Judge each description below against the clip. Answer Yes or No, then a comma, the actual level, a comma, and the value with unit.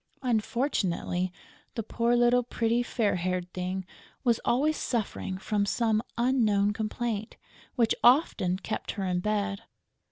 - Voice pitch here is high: Yes, high, 215 Hz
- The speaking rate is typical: No, slow, 125 wpm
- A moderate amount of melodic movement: Yes, average, 3.9 semitones